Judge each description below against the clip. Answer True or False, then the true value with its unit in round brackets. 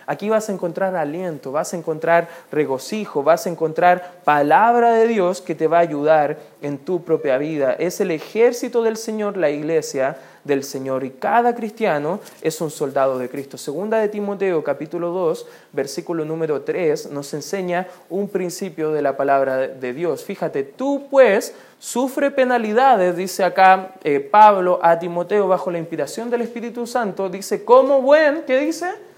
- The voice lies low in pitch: False (180 Hz)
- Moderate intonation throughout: False (6.6 semitones)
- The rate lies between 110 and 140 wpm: False (165 wpm)